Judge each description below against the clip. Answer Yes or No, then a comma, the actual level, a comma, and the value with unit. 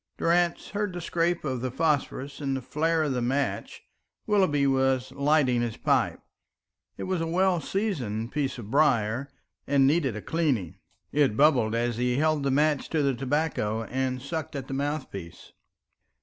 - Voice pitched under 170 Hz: Yes, medium, 140 Hz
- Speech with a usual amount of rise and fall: Yes, average, 4.1 semitones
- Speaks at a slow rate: No, average, 165 wpm